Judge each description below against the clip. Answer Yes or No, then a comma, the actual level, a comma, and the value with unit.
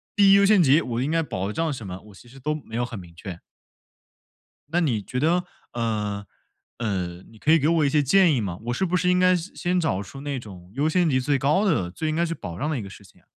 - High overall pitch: No, medium, 140 Hz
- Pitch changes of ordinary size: No, wide, 7.8 semitones